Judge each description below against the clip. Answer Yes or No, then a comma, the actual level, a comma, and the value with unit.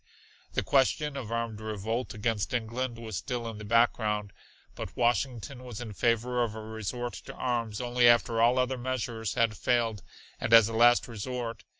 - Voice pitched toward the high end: No, low, 115 Hz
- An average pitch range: No, narrow, 1.8 semitones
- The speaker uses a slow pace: No, average, 175 wpm